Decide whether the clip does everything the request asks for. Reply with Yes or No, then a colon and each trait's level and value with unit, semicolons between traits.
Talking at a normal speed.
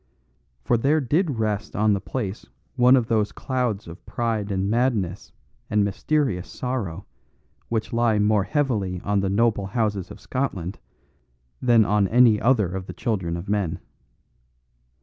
Yes: average, 150 wpm